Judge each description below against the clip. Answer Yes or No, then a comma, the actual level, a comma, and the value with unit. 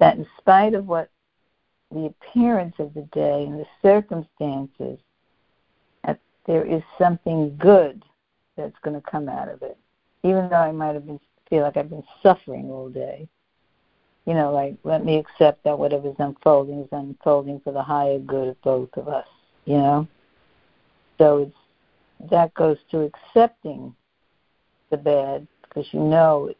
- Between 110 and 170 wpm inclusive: Yes, average, 160 wpm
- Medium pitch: Yes, medium, 150 Hz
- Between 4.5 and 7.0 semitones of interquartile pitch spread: No, narrow, 2.5 semitones